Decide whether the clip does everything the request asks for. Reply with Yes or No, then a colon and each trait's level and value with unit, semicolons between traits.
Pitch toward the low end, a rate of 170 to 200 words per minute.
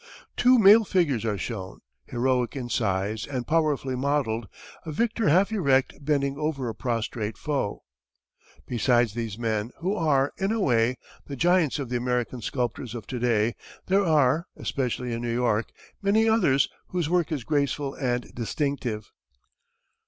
No: low, 130 Hz; average, 150 wpm